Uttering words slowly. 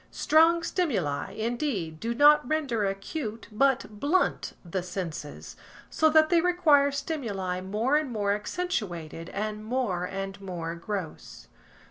Yes: slow, 125 wpm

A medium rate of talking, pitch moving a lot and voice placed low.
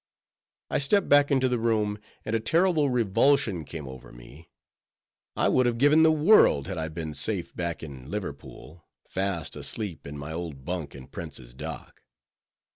Yes: average, 165 wpm; wide, 8.9 semitones; very low, 95 Hz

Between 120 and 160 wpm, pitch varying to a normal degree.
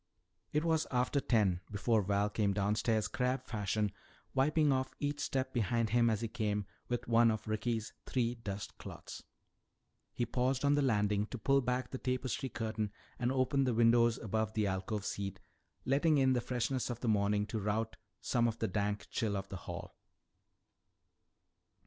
No: average, 170 wpm; average, 3.5 semitones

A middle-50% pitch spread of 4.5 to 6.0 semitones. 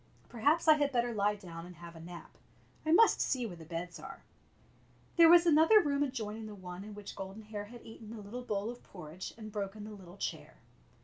Yes: average, 4.9 semitones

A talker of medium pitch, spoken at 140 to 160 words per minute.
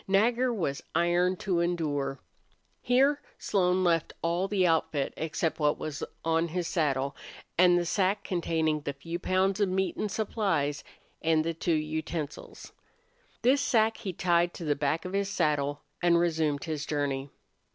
Yes: medium, 170 Hz; average, 155 wpm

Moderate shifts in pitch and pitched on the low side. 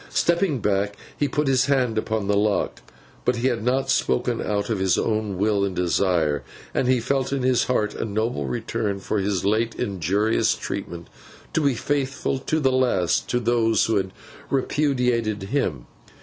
Yes: average, 4.6 semitones; low, 110 Hz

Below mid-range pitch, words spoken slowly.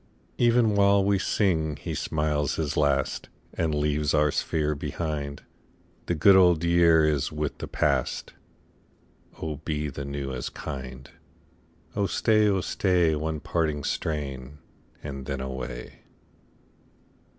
Yes: very low, 75 Hz; slow, 130 wpm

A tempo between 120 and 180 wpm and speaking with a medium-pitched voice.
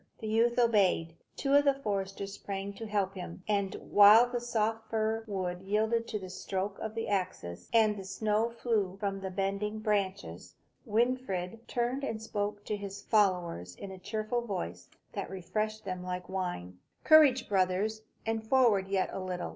No: average, 170 wpm; high, 205 Hz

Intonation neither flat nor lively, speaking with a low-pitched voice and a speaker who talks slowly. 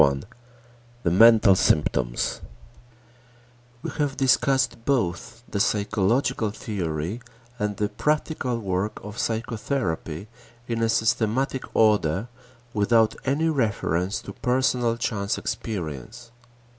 Yes: average, 4.2 semitones; low, 110 Hz; slow, 100 wpm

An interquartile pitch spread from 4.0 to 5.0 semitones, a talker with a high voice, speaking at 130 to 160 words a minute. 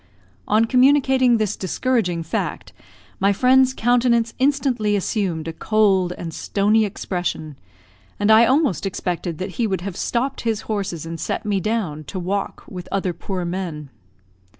Yes: average, 4.7 semitones; high, 205 Hz; average, 150 wpm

